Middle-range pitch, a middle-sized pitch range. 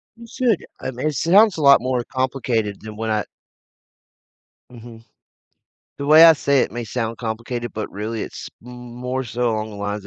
No: low, 120 Hz; average, 3.8 semitones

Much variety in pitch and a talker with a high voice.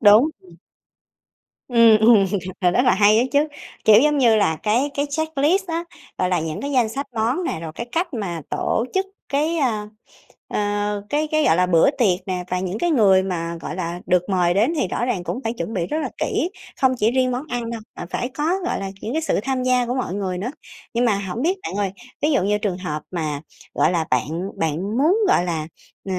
Yes: wide, 6.6 semitones; high, 220 Hz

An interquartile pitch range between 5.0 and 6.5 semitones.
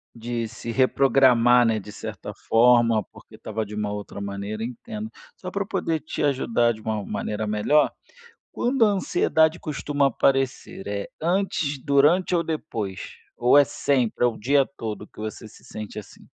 Yes: wide, 5.5 semitones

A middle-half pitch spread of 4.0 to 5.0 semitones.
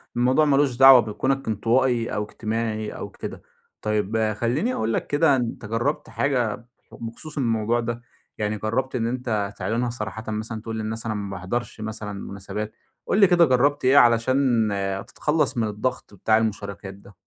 No: average, 3.1 semitones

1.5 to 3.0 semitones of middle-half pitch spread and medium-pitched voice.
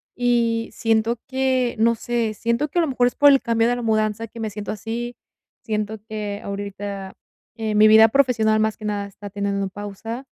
No: narrow, 2.4 semitones; high, 220 Hz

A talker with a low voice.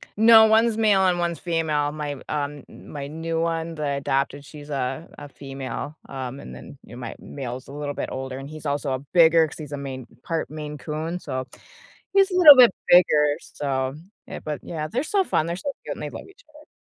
No: medium, 150 Hz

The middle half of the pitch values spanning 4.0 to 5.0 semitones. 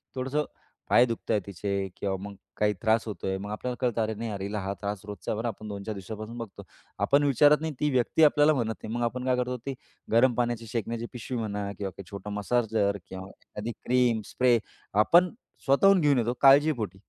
No: average, 3.6 semitones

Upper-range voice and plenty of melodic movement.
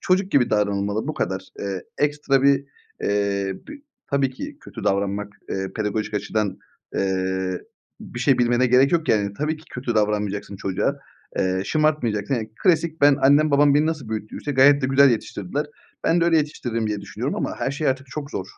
No: low, 120 Hz; wide, 6.1 semitones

